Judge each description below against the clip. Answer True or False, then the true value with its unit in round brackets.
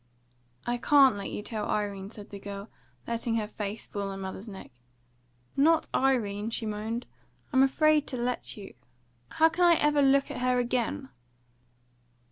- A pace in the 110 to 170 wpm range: True (165 wpm)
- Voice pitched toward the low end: False (230 Hz)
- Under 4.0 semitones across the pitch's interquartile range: False (4.7 semitones)